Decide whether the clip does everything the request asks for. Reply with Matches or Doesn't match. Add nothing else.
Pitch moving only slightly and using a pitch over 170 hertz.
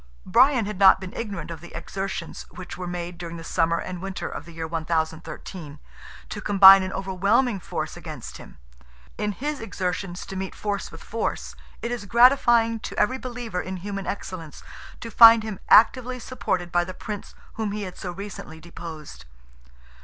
Doesn't match